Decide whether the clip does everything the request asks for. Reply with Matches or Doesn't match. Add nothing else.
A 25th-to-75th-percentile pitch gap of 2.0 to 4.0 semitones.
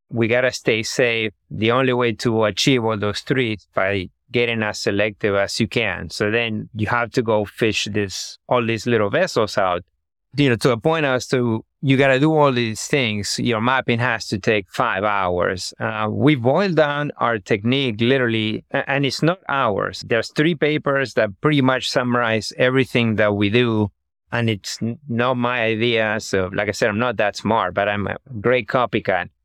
Matches